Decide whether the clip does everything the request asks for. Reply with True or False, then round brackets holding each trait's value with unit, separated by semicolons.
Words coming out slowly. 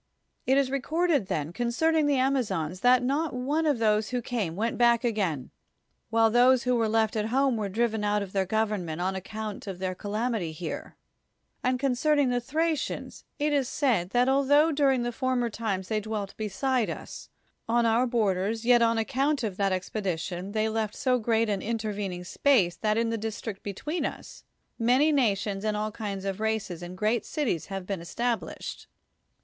False (180 wpm)